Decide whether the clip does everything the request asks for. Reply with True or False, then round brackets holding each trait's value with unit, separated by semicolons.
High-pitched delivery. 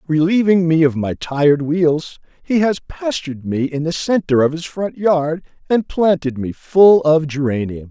False (160 Hz)